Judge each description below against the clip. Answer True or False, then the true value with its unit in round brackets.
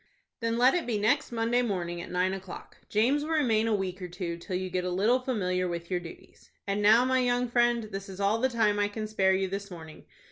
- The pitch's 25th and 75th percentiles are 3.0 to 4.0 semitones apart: False (4.5 semitones)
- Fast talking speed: True (245 wpm)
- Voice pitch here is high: True (205 Hz)